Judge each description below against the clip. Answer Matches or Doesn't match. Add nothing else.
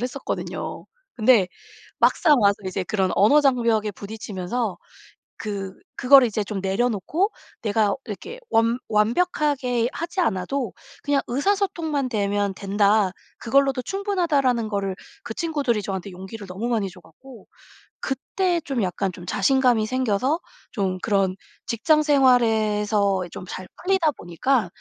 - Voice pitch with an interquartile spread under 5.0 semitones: Doesn't match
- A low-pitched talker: Doesn't match